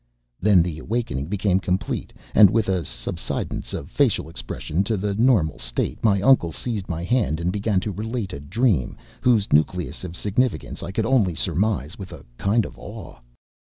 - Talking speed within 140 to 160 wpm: No, average, 175 wpm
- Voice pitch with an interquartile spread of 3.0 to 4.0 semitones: No, average, 4.7 semitones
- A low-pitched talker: Yes, very low, 95 Hz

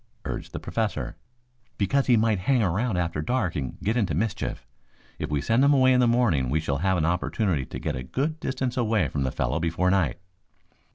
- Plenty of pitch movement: Yes, wide, 7.4 semitones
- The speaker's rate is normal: No, fast, 210 wpm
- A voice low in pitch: Yes, very low, 95 Hz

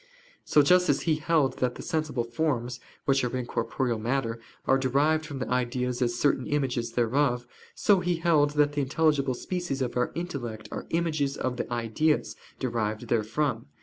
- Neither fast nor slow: Yes, average, 175 wpm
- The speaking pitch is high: No, low, 135 Hz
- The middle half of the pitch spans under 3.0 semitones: No, average, 4.0 semitones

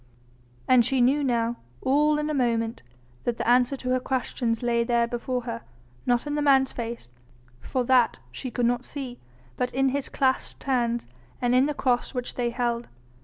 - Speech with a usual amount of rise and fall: No, narrow, 1.9 semitones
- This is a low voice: No, very high, 250 Hz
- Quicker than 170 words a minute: Yes, average, 185 wpm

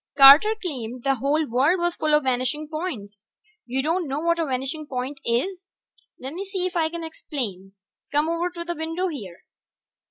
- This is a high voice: Yes, very high, 300 Hz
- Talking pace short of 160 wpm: No, average, 180 wpm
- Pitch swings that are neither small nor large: Yes, average, 4.8 semitones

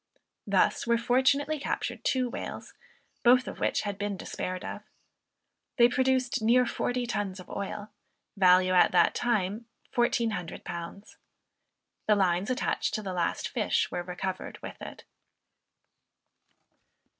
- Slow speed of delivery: Yes, slow, 125 wpm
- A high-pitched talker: Yes, high, 215 Hz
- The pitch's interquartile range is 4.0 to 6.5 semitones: Yes, average, 4.7 semitones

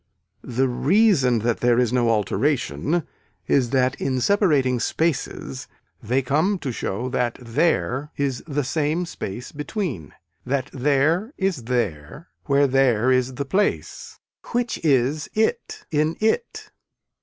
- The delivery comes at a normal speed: No, slow, 130 wpm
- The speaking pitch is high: No, low, 135 Hz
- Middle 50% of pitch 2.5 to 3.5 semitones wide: No, average, 4.5 semitones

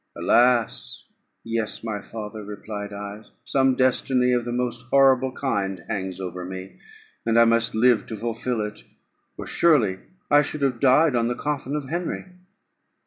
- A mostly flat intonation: No, average, 3.7 semitones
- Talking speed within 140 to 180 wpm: Yes, average, 155 wpm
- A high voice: No, low, 115 Hz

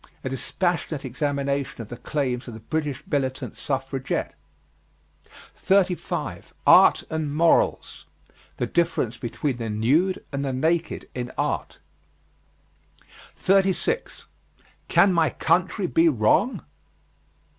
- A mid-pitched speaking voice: Yes, medium, 145 Hz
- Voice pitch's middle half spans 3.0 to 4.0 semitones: No, average, 4.8 semitones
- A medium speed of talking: No, slow, 105 wpm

